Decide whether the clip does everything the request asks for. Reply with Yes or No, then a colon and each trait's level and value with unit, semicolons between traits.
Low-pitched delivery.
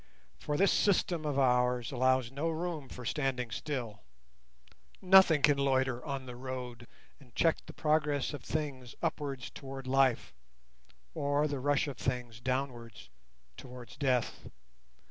Yes: low, 130 Hz